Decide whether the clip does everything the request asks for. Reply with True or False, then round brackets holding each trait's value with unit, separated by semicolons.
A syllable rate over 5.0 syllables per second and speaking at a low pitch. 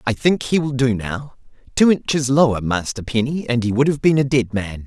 True (5.3 syllables/s; 125 Hz)